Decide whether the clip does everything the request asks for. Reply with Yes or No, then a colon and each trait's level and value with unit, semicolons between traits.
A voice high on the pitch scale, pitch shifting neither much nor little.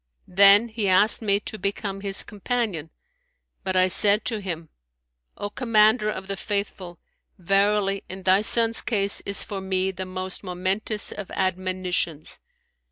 No: high, 195 Hz; narrow, 2.1 semitones